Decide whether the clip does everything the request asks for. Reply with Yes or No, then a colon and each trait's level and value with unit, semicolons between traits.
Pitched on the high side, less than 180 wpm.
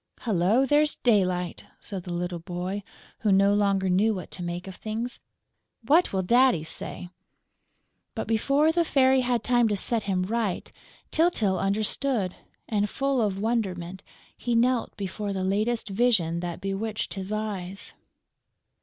Yes: high, 205 Hz; average, 145 wpm